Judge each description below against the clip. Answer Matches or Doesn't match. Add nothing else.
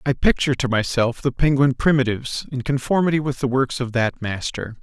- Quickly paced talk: Doesn't match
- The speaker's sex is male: Matches